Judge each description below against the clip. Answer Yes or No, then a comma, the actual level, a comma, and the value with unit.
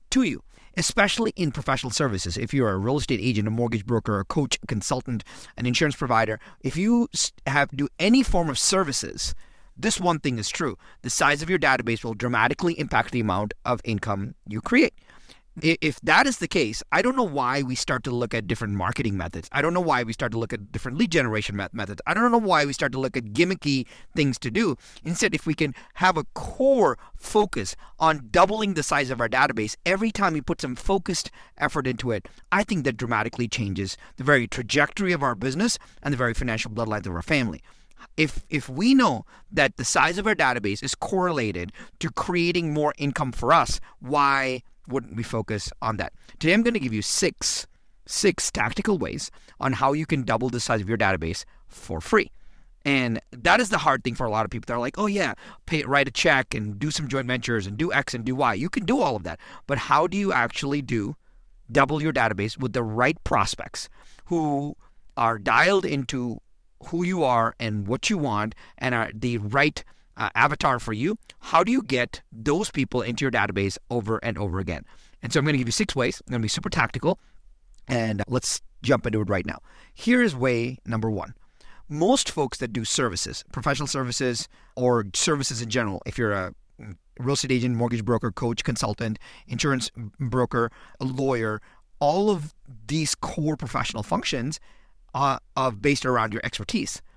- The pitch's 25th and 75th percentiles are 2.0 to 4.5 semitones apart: No, average, 5.0 semitones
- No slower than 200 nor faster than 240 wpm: Yes, fast, 205 wpm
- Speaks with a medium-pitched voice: No, low, 130 Hz